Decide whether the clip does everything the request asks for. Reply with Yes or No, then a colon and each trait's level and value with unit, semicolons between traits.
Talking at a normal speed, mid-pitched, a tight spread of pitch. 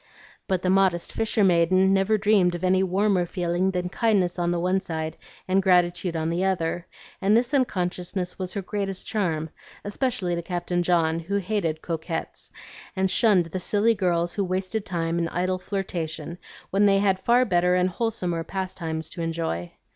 Yes: average, 170 wpm; medium, 180 Hz; narrow, 2.2 semitones